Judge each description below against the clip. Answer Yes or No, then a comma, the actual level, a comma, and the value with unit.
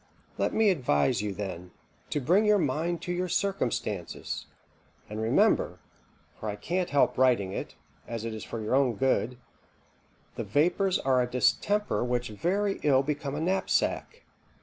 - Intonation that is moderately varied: No, wide, 7.9 semitones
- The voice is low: Yes, low, 130 Hz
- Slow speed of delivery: No, average, 155 wpm